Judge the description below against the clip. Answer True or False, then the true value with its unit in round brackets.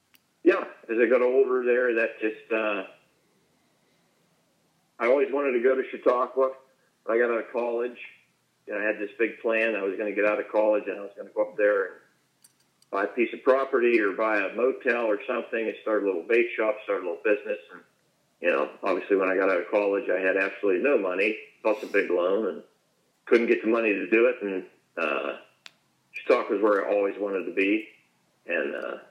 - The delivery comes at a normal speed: False (215 wpm)